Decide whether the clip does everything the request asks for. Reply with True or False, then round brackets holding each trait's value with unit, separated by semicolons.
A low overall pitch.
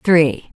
False (160 Hz)